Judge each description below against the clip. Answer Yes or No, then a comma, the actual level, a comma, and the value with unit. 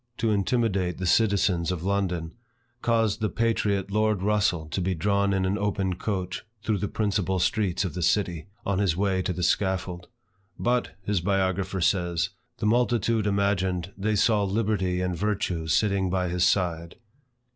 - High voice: No, very low, 95 Hz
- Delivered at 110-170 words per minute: Yes, average, 160 wpm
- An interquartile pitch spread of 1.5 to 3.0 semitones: Yes, narrow, 2.4 semitones